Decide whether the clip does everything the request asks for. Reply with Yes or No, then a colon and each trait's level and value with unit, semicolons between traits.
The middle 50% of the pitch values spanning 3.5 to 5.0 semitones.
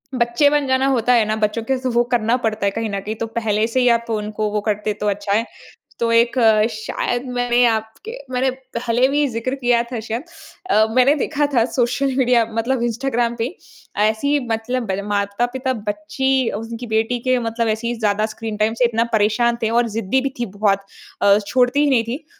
No: narrow, 2.5 semitones